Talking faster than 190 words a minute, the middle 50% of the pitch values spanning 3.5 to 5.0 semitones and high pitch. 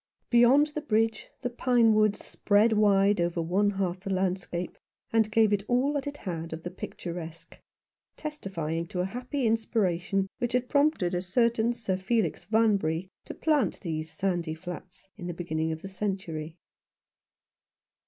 No: average, 155 wpm; average, 4.7 semitones; high, 195 Hz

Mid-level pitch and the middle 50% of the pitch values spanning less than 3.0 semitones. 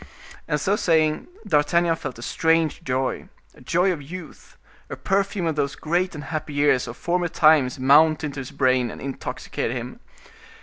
No: medium, 155 Hz; average, 3.6 semitones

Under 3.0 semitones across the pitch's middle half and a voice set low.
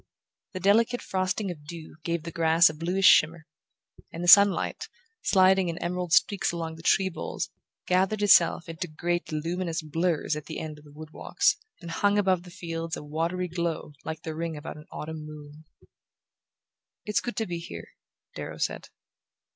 No: narrow, 2.6 semitones; medium, 170 Hz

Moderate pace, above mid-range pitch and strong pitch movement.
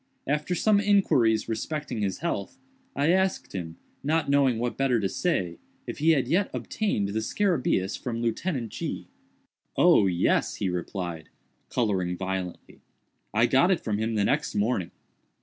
No: average, 150 wpm; low, 115 Hz; wide, 8.1 semitones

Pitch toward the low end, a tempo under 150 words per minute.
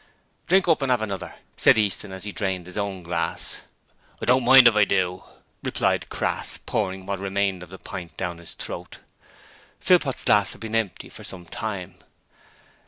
No: low, 100 Hz; average, 175 wpm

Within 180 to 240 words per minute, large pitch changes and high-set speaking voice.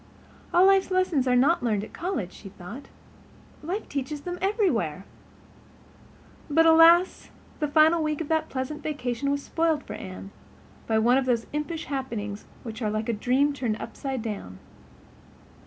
No: average, 155 wpm; wide, 6.2 semitones; very high, 280 Hz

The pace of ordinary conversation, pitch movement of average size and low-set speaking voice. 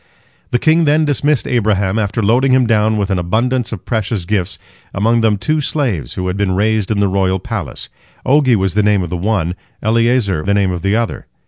No: fast, 210 wpm; average, 4.0 semitones; low, 105 Hz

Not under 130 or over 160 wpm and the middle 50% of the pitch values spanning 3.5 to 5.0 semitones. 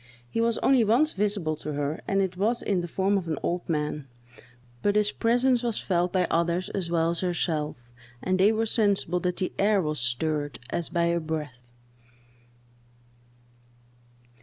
No: average, 170 wpm; average, 4.6 semitones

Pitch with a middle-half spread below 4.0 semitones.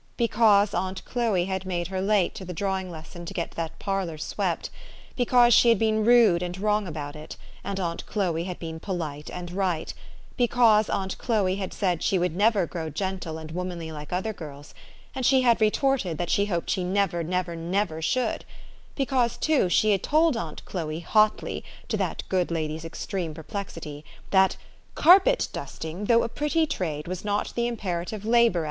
No: average, 4.3 semitones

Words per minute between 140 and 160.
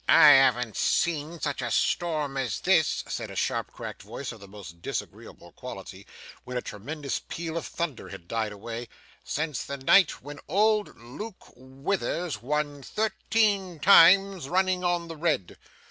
Yes: average, 150 wpm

